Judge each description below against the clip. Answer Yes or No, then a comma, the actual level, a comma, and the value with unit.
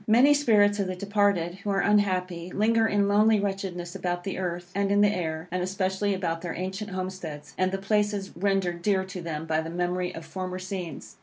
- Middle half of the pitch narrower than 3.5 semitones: Yes, narrow, 2.4 semitones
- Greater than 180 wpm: Yes, fast, 205 wpm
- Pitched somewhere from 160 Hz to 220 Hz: Yes, high, 190 Hz